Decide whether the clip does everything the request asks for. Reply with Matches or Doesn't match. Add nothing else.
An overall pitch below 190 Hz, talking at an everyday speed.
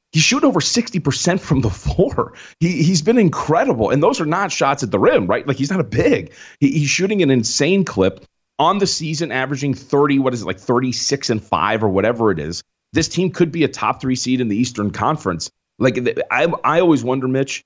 Doesn't match